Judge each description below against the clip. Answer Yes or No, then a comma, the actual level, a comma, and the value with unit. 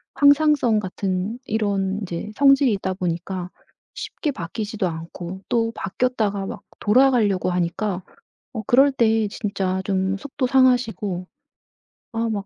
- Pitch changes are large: No, average, 4.6 semitones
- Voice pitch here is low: No, high, 210 Hz